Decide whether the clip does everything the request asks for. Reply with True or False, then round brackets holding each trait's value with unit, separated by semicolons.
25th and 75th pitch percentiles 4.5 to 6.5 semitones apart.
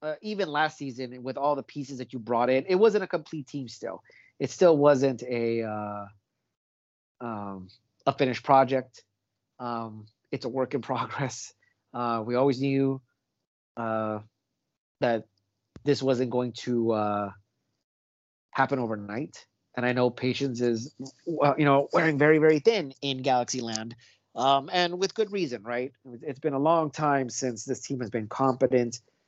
False (3.5 semitones)